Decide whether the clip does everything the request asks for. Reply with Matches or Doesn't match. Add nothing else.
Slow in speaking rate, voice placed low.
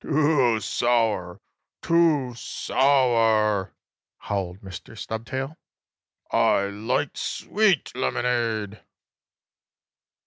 Matches